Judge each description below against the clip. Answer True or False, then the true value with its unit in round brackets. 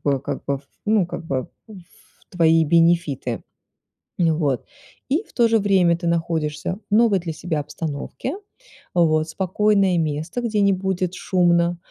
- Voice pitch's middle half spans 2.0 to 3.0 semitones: False (3.6 semitones)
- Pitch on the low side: False (170 Hz)